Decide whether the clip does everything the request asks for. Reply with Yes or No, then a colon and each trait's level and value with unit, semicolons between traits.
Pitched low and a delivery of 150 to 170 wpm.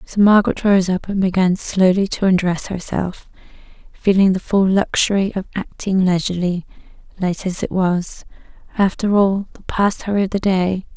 No: high, 190 Hz; average, 160 wpm